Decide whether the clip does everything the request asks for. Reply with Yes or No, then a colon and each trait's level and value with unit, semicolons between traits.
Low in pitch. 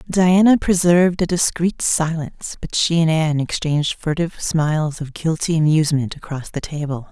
No: medium, 165 Hz